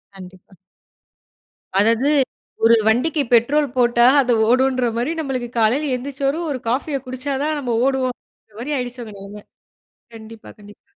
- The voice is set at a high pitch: Yes, very high, 250 Hz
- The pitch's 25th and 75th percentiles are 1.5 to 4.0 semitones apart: Yes, average, 3.3 semitones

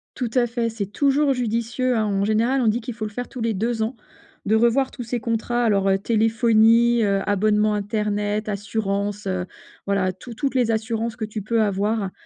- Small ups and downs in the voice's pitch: Yes, narrow, 2.3 semitones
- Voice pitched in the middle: No, high, 220 Hz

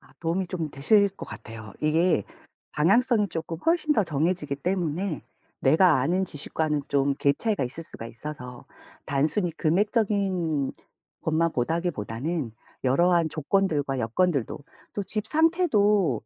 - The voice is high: No, medium, 165 Hz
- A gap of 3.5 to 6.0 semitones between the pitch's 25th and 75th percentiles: Yes, wide, 5.5 semitones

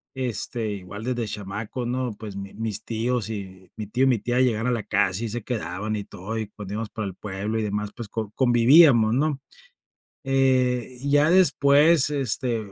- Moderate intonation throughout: Yes, average, 3.6 semitones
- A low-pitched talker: Yes, low, 115 Hz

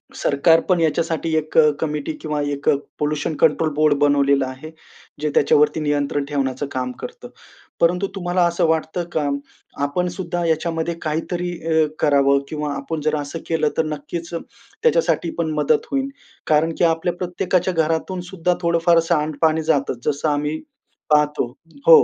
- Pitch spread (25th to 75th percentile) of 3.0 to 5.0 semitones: No, narrow, 2.4 semitones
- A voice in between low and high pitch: Yes, medium, 155 Hz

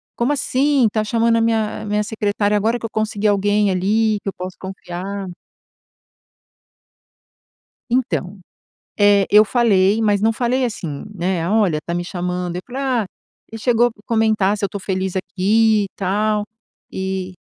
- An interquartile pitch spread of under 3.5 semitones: Yes, average, 2.8 semitones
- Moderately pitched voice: No, high, 210 Hz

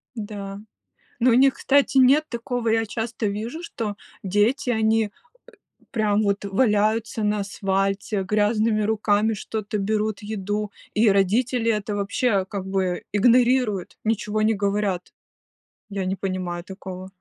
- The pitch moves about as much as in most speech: No, narrow, 2.3 semitones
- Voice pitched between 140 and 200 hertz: No, high, 210 Hz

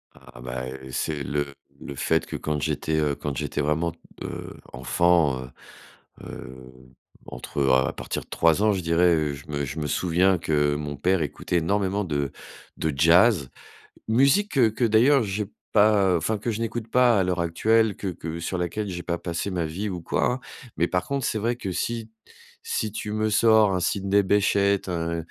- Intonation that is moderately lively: No, wide, 5.7 semitones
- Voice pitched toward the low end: Yes, very low, 90 Hz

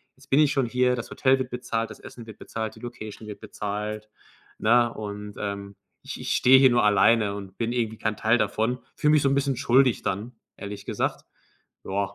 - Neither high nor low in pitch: No, low, 115 Hz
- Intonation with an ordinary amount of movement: Yes, average, 3.3 semitones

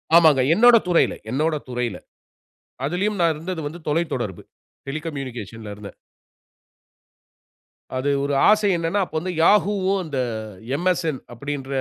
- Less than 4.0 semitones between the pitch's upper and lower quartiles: No, average, 5.2 semitones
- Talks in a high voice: No, medium, 155 Hz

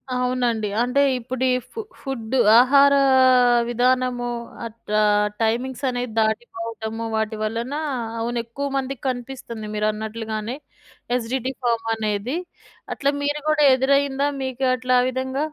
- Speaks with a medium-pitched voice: No, high, 245 Hz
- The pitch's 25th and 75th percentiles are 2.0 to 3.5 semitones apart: Yes, narrow, 2.5 semitones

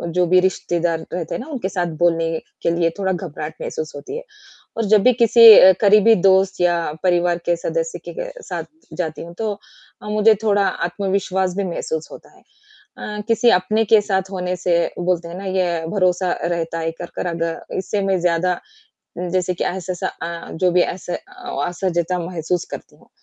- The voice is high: No, medium, 180 Hz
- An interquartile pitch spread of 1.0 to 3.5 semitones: Yes, narrow, 2.6 semitones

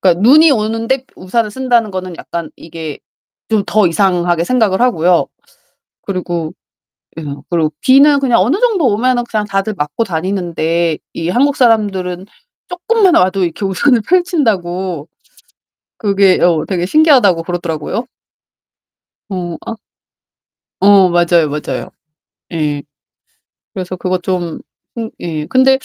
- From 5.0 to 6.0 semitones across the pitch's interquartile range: Yes, wide, 5.6 semitones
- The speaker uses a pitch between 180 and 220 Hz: Yes, high, 190 Hz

